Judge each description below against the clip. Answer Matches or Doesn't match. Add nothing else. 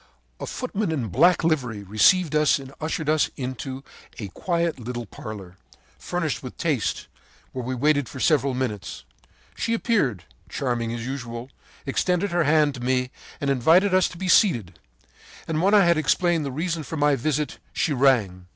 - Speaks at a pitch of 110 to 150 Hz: Matches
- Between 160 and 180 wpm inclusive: Matches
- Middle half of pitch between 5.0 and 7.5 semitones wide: Matches